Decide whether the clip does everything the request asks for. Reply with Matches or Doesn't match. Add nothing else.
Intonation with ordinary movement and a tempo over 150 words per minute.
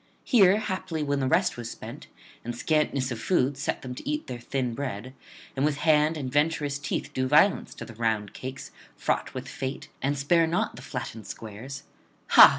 Matches